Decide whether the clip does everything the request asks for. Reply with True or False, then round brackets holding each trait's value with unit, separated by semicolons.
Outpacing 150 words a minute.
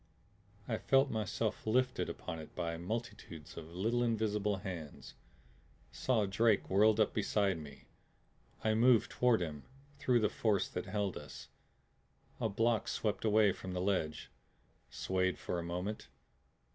False (140 wpm)